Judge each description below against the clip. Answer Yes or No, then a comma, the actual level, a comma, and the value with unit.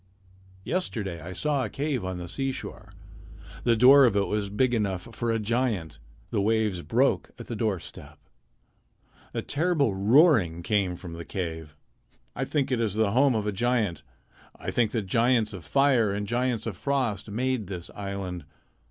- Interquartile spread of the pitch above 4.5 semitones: Yes, average, 4.9 semitones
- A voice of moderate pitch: No, low, 110 Hz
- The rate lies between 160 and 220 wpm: Yes, average, 170 wpm